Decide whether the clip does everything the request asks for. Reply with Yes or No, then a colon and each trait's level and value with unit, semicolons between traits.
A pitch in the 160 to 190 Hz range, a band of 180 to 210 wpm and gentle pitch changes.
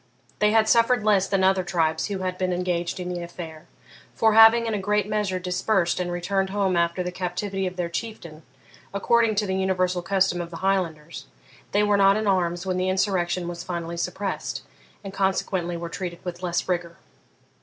Yes: medium, 185 Hz; average, 190 wpm; narrow, 2.3 semitones